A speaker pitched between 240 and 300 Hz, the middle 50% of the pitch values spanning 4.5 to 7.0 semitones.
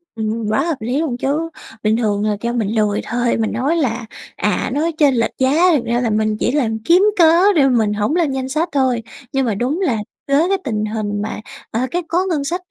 Yes: high, 245 Hz; wide, 5.6 semitones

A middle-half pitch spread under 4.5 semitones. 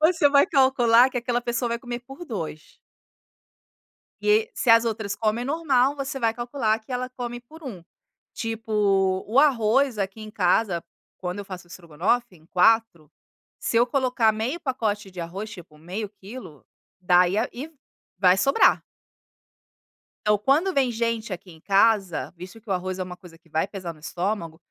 No: average, 5.0 semitones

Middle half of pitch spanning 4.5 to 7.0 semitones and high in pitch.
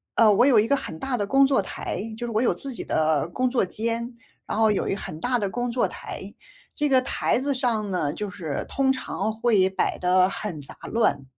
Yes: average, 5.0 semitones; high, 225 Hz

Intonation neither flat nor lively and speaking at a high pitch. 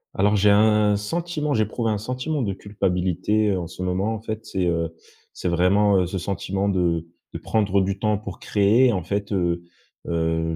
No: average, 3.0 semitones; low, 100 Hz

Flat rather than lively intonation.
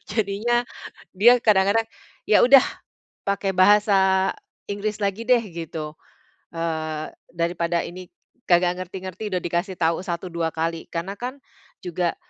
No: average, 3.5 semitones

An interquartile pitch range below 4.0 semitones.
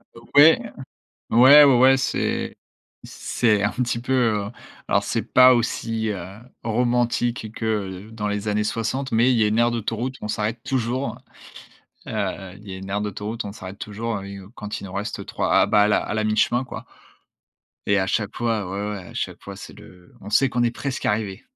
Yes: average, 2.8 semitones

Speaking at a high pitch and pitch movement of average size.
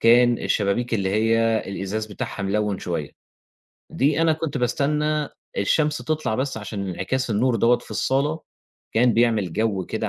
No: low, 115 Hz; average, 4.9 semitones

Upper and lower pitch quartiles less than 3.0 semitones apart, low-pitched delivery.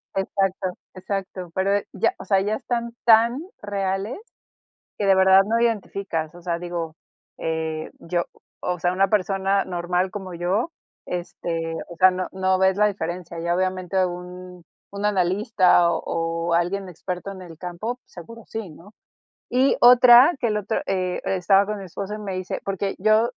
No: narrow, 2.5 semitones; high, 190 Hz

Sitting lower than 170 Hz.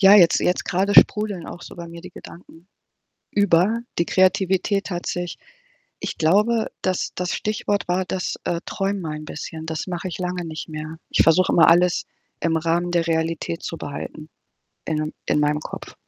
No: medium, 175 Hz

